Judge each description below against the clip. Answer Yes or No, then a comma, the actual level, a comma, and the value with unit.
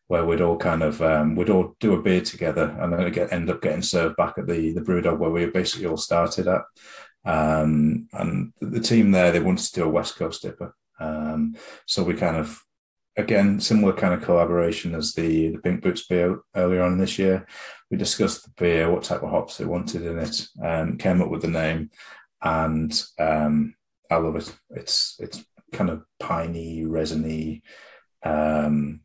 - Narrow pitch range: Yes, narrow, 2.2 semitones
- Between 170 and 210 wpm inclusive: Yes, average, 195 wpm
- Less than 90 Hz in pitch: Yes, very low, 80 Hz